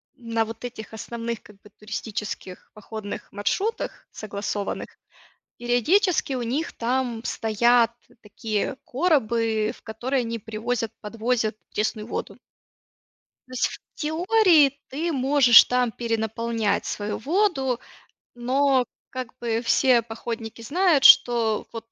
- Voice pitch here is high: Yes, high, 235 Hz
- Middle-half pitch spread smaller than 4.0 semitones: Yes, average, 3.1 semitones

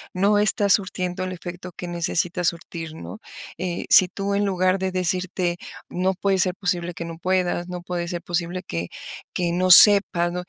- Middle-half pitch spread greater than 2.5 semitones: No, narrow, 1.4 semitones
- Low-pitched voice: No, medium, 180 Hz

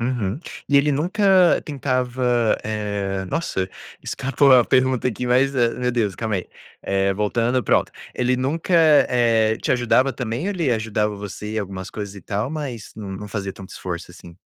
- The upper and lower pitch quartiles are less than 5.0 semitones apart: Yes, average, 4.2 semitones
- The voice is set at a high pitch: No, low, 120 Hz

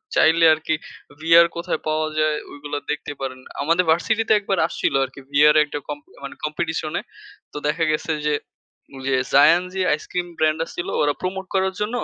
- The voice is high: No, medium, 160 Hz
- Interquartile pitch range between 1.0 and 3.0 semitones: No, average, 3.4 semitones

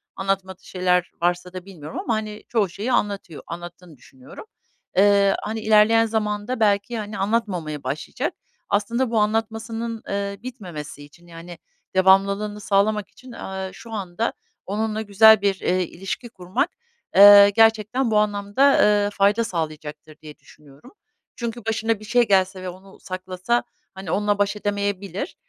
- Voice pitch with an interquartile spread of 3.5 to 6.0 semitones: No, average, 3.0 semitones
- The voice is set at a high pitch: Yes, high, 200 Hz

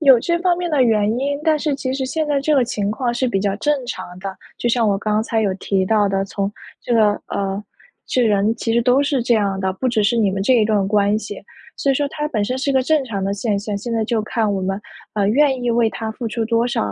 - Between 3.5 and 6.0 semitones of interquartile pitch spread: Yes, average, 4.2 semitones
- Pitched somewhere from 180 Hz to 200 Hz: No, high, 225 Hz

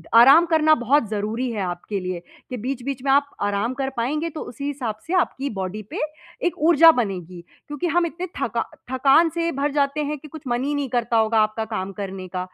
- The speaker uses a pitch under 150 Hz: No, very high, 260 Hz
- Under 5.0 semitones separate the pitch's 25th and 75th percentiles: No, wide, 5.6 semitones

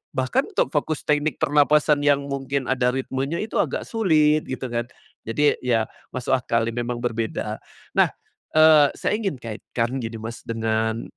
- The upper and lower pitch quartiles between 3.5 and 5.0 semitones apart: Yes, average, 4.2 semitones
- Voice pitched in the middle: No, low, 130 Hz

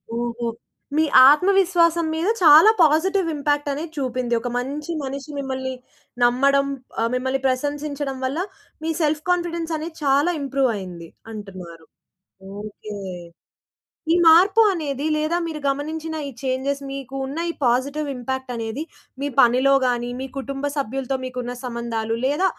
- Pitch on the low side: No, very high, 275 Hz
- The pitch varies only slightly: No, average, 3.8 semitones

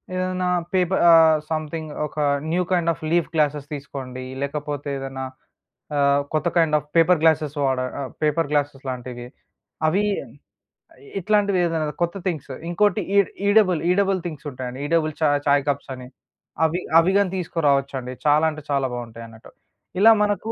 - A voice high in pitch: No, medium, 155 Hz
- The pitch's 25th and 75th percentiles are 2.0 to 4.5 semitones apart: Yes, average, 3.9 semitones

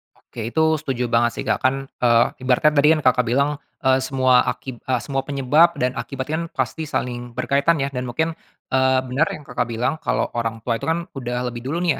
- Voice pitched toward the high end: No, low, 130 Hz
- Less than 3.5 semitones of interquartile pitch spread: Yes, average, 2.9 semitones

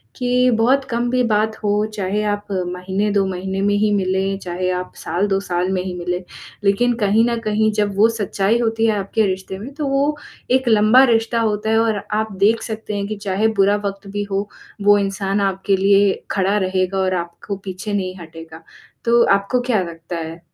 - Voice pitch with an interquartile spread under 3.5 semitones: Yes, average, 2.7 semitones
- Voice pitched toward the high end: Yes, high, 205 Hz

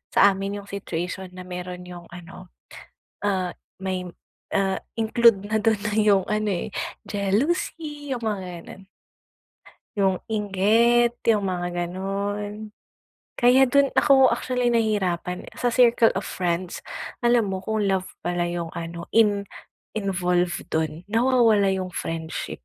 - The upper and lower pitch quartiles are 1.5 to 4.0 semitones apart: Yes, average, 3.7 semitones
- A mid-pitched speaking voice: No, high, 200 Hz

